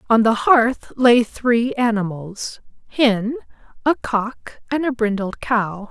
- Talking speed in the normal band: No, slow, 130 wpm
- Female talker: Yes, female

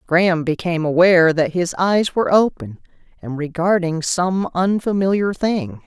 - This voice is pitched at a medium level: Yes, medium, 175 Hz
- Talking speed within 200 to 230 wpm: No, slow, 135 wpm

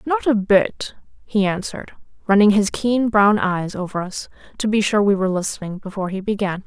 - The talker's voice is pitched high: Yes, high, 205 Hz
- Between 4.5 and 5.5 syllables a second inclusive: Yes, 5.4 syllables/s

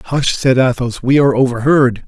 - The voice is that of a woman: No, male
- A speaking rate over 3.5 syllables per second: Yes, 5.5 syllables/s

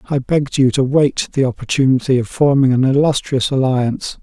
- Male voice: Yes, male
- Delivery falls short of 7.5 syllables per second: Yes, 5.6 syllables/s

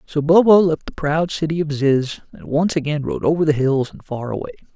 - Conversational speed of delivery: No, fast, 225 wpm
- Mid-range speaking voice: Yes, medium, 155 Hz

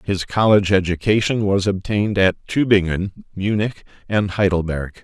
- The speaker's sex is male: Yes, male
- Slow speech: Yes, slow, 120 wpm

